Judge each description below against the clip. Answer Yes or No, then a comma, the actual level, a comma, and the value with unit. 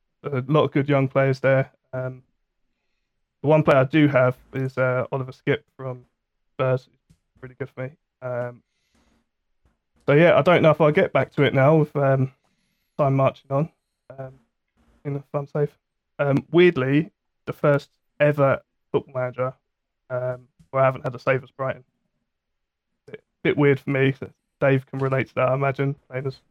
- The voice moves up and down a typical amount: No, narrow, 1.8 semitones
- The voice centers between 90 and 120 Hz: No, low, 135 Hz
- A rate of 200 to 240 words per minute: No, average, 170 wpm